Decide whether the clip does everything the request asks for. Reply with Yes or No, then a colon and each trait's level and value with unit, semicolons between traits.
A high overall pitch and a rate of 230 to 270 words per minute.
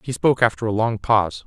No: low, 110 Hz; fast, 245 wpm